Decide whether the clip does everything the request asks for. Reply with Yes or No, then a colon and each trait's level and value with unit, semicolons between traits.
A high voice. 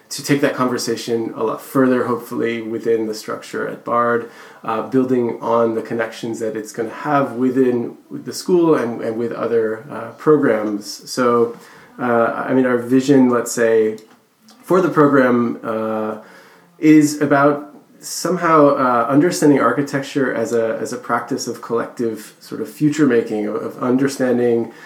No: low, 120 Hz